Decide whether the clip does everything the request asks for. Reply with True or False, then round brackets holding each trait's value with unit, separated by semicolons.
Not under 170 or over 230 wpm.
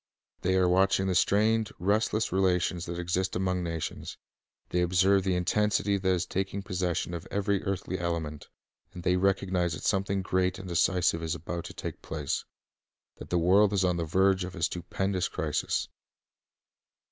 True (180 wpm)